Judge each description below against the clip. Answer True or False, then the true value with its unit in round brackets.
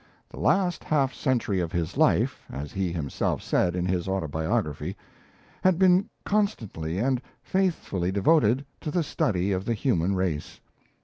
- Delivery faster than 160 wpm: False (145 wpm)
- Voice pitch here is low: True (95 Hz)